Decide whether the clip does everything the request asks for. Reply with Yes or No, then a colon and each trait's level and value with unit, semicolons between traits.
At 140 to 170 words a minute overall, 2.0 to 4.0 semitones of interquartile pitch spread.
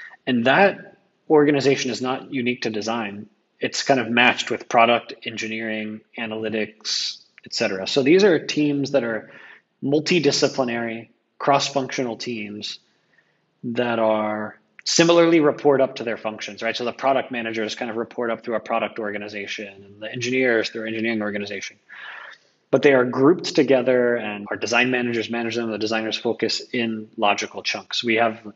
Yes: average, 155 wpm; average, 3.4 semitones